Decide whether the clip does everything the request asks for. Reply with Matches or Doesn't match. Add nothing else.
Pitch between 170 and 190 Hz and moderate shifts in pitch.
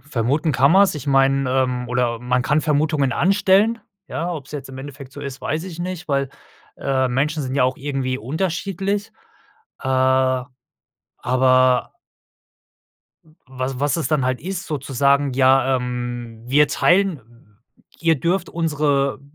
Doesn't match